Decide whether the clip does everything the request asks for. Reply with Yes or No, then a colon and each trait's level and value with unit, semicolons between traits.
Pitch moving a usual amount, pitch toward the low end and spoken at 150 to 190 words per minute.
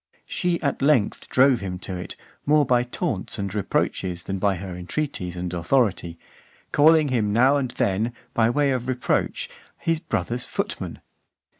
No: wide, 6.6 semitones; low, 115 Hz; average, 160 wpm